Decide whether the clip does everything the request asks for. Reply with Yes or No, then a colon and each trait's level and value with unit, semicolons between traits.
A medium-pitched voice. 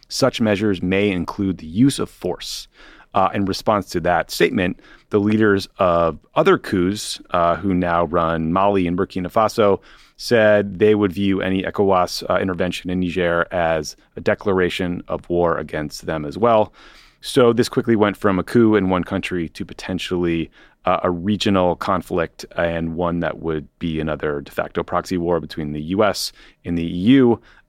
No: very low, 90 Hz